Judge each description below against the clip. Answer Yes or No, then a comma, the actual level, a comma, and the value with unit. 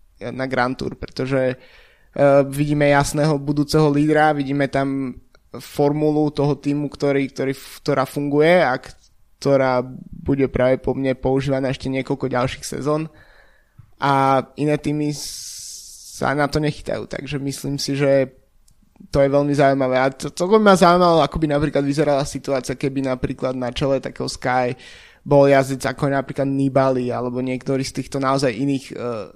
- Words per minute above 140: Yes, average, 150 wpm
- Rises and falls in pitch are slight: Yes, narrow, 1.6 semitones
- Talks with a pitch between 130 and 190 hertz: Yes, medium, 140 Hz